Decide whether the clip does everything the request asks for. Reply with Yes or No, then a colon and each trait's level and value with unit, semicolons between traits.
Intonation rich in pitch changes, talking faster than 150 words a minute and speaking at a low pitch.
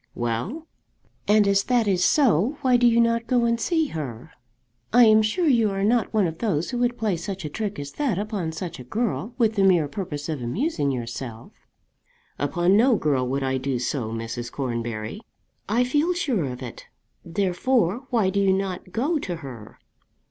No: wide, 8.6 semitones; average, 190 wpm; high, 195 Hz